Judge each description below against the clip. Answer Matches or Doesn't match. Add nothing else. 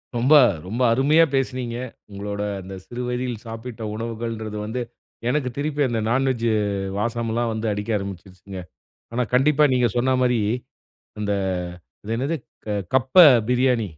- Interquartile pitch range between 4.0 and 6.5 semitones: Doesn't match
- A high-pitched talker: Doesn't match